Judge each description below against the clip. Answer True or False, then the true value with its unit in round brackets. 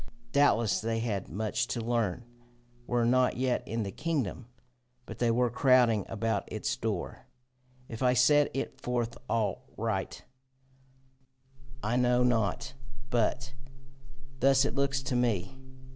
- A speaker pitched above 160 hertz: False (120 Hz)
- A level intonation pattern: True (2.3 semitones)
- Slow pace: True (130 wpm)